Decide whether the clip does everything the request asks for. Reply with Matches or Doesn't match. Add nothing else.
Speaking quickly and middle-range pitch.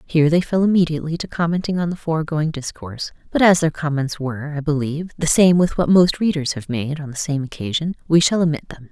Matches